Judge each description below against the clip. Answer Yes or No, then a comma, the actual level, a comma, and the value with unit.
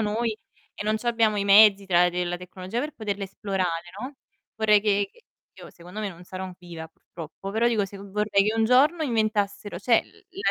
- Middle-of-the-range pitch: No, high, 205 Hz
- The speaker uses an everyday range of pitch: Yes, average, 3.1 semitones